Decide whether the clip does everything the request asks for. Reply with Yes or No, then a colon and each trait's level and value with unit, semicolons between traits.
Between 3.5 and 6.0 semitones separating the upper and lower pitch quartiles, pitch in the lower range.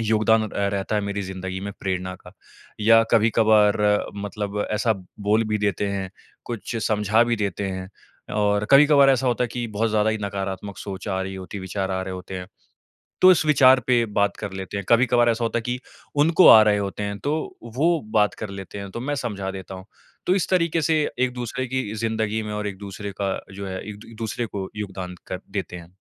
No: average, 3.1 semitones; low, 105 Hz